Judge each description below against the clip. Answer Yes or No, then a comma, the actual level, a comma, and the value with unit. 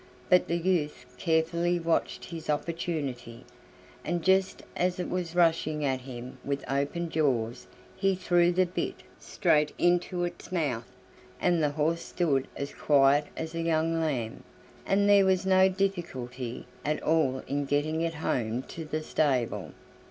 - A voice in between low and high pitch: Yes, medium, 160 Hz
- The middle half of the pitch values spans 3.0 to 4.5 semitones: Yes, average, 3.9 semitones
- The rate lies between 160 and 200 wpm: No, average, 150 wpm